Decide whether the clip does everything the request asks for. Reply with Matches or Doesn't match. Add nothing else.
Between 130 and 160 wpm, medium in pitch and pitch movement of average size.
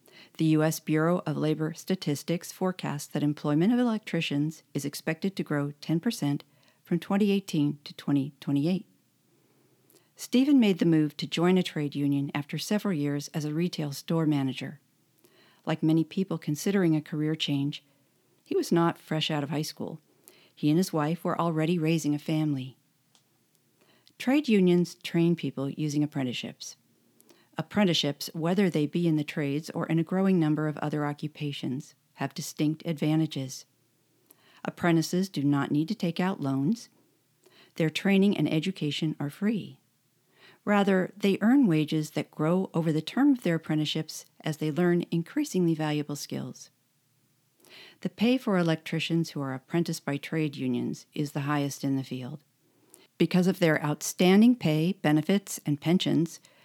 Matches